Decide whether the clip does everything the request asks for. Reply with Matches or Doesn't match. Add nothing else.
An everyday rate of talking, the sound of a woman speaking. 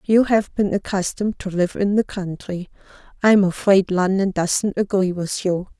Matches